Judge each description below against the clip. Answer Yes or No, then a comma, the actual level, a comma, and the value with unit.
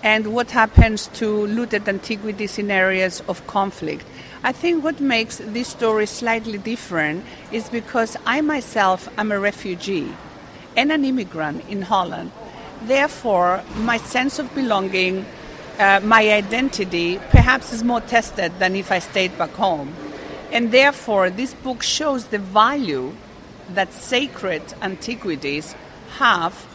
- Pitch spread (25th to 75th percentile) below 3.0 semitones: No, average, 3.8 semitones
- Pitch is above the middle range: Yes, high, 215 Hz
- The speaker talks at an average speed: No, slow, 130 wpm